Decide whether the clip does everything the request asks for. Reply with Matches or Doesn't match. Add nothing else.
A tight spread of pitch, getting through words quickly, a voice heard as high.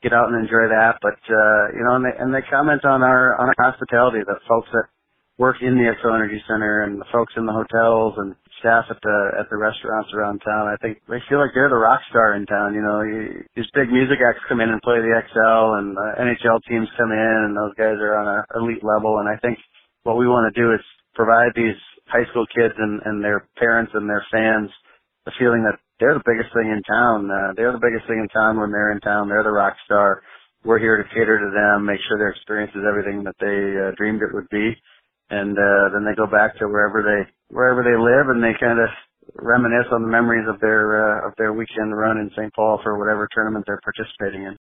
Doesn't match